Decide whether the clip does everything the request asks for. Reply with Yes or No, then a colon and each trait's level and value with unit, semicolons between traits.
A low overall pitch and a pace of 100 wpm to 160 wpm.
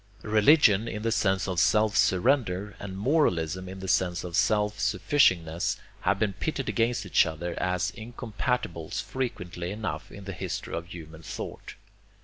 Yes: very low, 95 Hz; average, 150 wpm